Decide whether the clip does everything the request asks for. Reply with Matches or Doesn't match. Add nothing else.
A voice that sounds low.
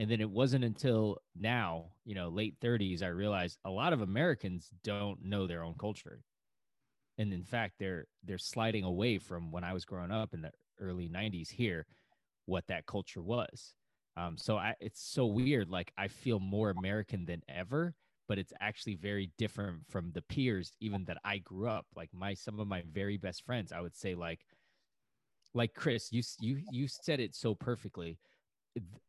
Matches